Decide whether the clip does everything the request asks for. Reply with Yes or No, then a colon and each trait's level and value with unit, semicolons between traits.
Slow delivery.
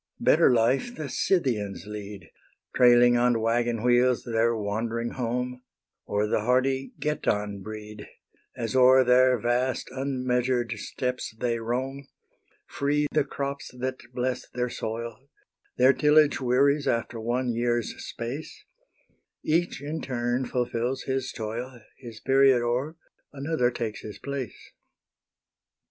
Yes: slow, 120 wpm